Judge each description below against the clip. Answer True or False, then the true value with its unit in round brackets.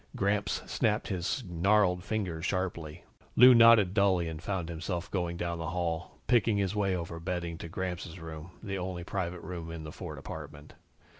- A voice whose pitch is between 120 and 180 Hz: False (90 Hz)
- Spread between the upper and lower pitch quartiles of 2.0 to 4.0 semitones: True (2.8 semitones)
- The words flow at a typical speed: True (170 wpm)